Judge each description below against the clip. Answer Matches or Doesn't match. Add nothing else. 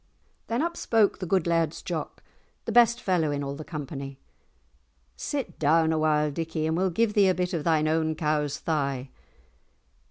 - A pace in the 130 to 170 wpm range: Doesn't match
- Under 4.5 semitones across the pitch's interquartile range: Matches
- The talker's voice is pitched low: Doesn't match